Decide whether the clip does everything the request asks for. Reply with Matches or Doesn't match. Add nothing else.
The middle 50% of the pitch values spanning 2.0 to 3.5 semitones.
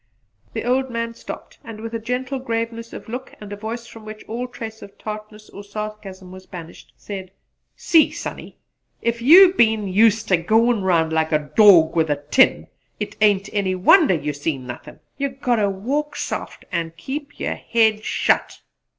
Doesn't match